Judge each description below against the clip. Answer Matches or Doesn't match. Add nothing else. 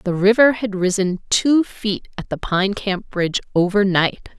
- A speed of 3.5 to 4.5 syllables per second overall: Matches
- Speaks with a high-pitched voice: Matches